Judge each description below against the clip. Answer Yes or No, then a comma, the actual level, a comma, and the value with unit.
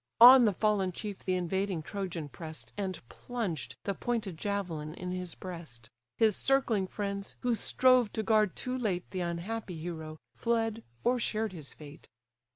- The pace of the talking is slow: No, average, 160 wpm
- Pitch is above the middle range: Yes, high, 195 Hz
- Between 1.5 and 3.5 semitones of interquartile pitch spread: No, average, 4.6 semitones